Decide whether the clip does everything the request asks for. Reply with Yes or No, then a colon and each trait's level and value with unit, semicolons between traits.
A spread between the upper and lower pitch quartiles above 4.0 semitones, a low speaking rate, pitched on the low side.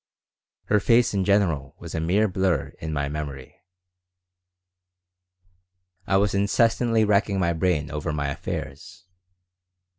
Yes: average, 5.1 semitones; slow, 120 wpm; very low, 90 Hz